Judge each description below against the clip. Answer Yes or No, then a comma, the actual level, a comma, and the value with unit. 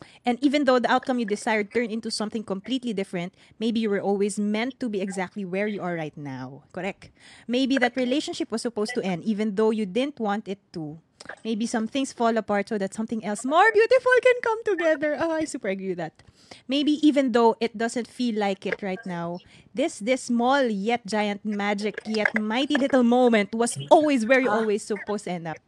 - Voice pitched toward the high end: Yes, high, 225 Hz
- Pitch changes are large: No, average, 4.2 semitones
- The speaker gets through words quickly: Yes, fast, 210 wpm